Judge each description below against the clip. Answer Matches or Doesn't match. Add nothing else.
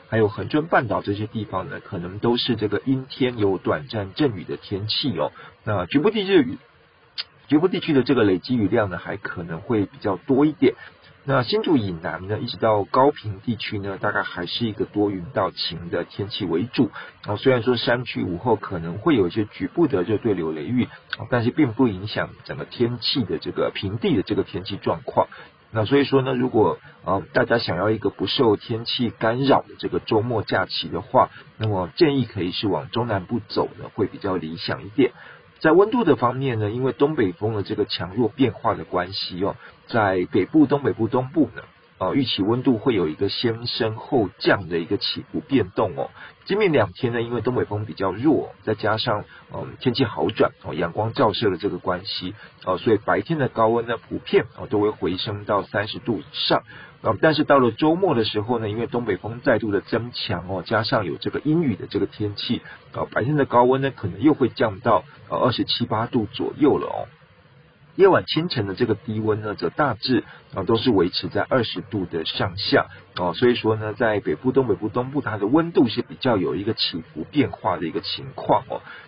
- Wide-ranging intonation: Doesn't match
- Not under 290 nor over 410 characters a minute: Matches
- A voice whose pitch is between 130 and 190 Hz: Doesn't match